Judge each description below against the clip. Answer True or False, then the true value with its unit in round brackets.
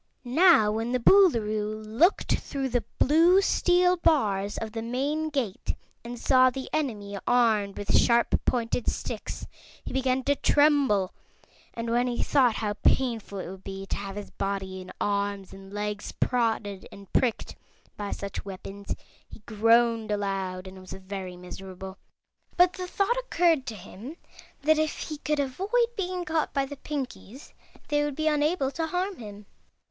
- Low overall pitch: False (235 Hz)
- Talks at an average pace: True (160 wpm)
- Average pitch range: False (6.6 semitones)